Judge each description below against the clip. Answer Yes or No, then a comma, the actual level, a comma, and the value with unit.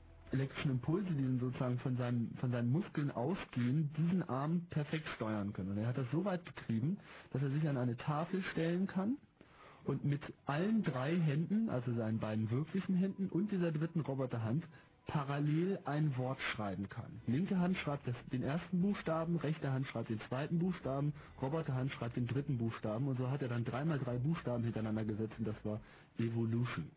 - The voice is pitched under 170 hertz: Yes, medium, 140 Hz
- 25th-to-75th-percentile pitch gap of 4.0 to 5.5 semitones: Yes, average, 5.2 semitones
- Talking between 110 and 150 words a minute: No, average, 175 wpm